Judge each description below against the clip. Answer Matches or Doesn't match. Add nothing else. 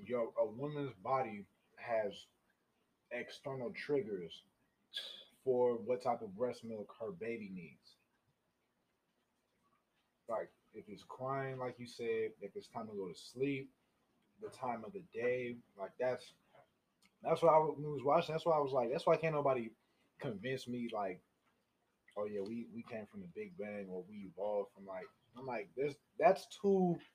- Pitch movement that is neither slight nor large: Doesn't match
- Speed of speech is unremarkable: Matches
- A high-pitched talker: Doesn't match